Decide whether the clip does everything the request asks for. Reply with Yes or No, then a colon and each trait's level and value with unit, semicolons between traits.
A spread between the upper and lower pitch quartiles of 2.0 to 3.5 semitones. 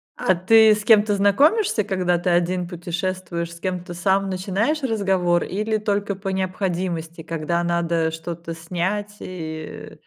Yes: average, 2.9 semitones